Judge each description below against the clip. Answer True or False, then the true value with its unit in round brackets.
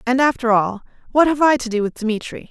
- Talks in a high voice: True (245 Hz)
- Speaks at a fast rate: True (240 wpm)